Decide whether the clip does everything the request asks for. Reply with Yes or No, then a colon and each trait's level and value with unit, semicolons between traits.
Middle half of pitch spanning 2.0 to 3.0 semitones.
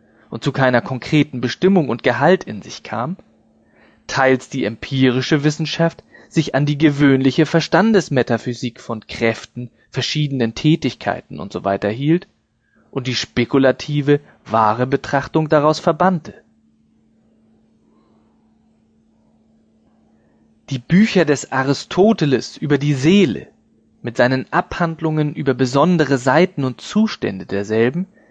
No: average, 5.2 semitones